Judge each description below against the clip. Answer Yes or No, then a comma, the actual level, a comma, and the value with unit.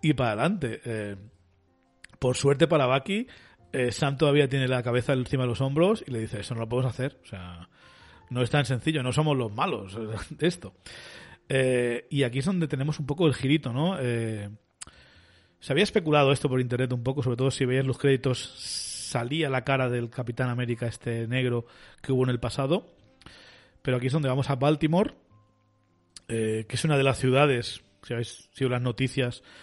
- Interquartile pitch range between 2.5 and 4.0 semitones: Yes, average, 3.3 semitones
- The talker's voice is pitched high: No, low, 125 Hz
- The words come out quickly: Yes, fast, 195 wpm